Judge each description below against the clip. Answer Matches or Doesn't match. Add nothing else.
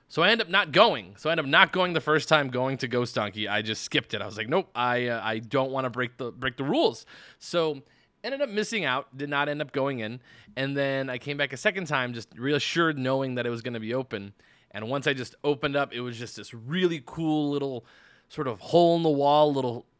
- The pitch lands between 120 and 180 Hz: Matches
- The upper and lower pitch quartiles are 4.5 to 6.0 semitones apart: Doesn't match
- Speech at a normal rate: Doesn't match